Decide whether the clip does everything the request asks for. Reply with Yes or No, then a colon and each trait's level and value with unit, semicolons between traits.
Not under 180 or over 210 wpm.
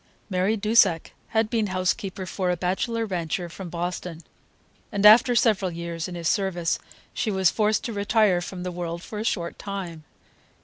No: average, 170 wpm